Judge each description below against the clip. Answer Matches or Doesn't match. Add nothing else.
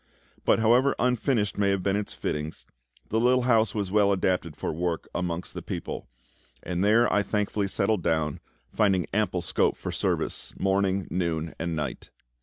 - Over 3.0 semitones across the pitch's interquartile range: Matches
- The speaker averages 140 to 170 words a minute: Matches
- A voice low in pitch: Matches